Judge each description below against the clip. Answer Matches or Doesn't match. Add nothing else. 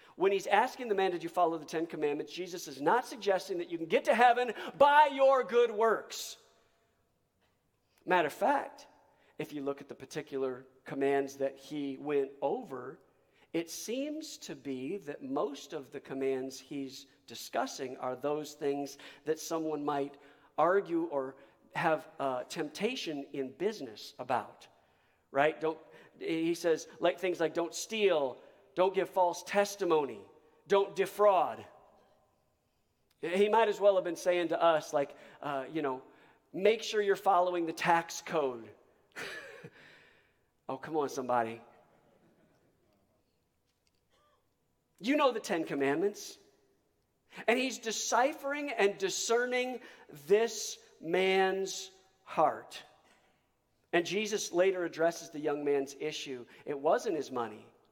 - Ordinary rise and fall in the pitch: Doesn't match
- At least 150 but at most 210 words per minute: Doesn't match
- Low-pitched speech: Doesn't match